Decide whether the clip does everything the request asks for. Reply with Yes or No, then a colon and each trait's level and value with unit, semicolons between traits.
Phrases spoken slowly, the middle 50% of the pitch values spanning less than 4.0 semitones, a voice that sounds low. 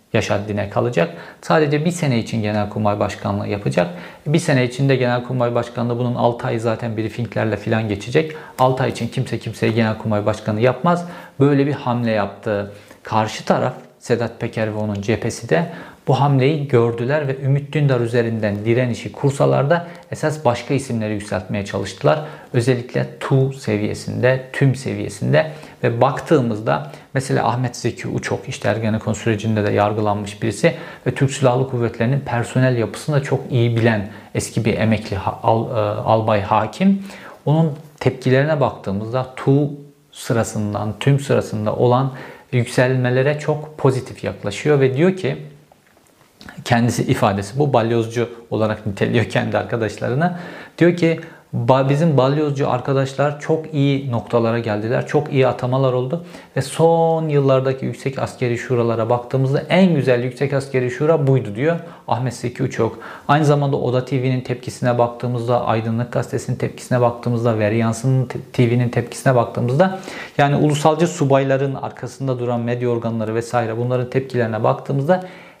No: average, 135 wpm; average, 3.6 semitones; low, 125 Hz